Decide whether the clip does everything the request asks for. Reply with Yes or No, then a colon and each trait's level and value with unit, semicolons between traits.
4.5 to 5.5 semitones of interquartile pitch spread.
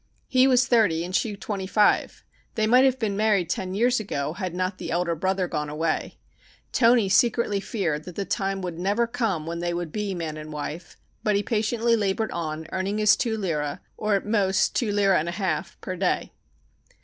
No: average, 4.0 semitones